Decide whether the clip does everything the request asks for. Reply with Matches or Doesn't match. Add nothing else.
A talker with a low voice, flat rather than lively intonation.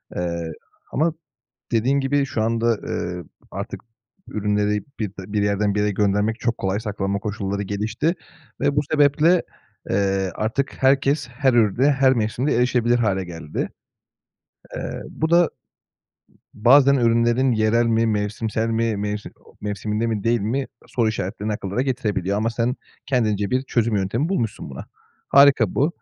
Doesn't match